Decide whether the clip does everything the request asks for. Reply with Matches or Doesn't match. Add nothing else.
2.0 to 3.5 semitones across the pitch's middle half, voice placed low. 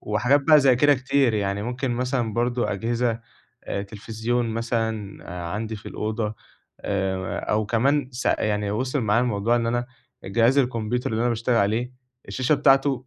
Matches